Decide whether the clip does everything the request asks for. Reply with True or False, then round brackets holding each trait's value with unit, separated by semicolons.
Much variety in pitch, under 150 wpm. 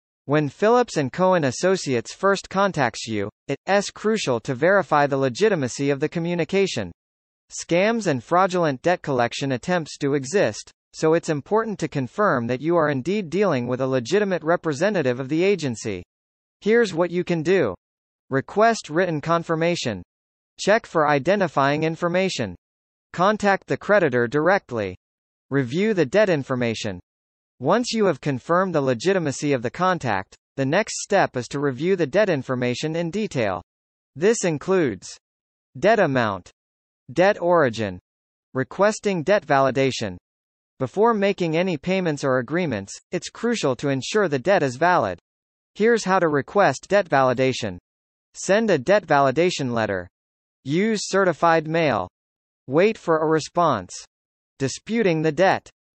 True (6.9 semitones; 135 wpm)